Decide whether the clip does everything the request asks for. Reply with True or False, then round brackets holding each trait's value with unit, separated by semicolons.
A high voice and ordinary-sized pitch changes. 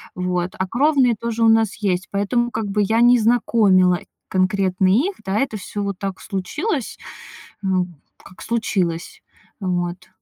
True (200 Hz; 4.0 semitones)